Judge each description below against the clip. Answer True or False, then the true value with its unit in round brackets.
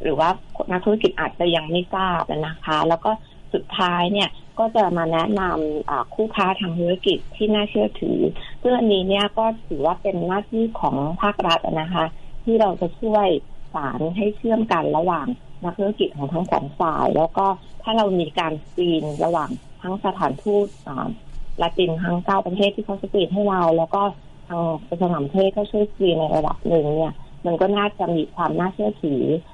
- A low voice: False (180 Hz)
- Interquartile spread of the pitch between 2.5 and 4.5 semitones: True (3.9 semitones)